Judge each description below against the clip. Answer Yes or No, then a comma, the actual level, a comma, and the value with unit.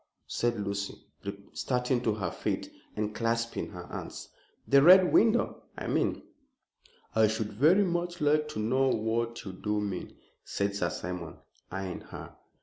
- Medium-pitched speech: No, low, 115 Hz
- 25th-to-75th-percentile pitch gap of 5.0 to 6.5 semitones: Yes, wide, 5.5 semitones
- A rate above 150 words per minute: No, average, 145 wpm